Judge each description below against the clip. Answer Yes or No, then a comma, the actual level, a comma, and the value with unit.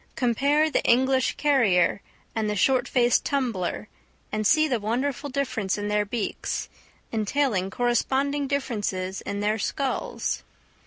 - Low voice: No, high, 240 Hz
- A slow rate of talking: Yes, slow, 125 wpm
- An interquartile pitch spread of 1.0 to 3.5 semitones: No, average, 4.9 semitones